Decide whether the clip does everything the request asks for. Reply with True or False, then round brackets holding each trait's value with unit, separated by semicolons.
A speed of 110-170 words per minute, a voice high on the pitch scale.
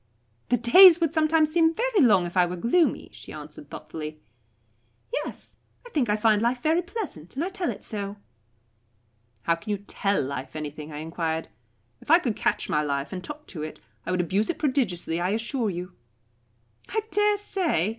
False (185 wpm; 215 Hz)